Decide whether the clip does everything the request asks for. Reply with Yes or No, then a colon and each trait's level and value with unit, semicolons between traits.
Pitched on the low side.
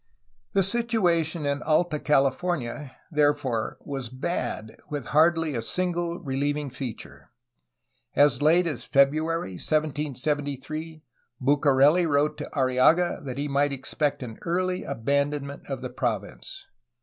No: medium, 145 Hz